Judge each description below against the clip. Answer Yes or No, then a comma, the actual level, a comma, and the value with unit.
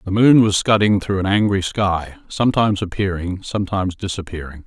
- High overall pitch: No, very low, 95 Hz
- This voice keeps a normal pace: Yes, average, 155 wpm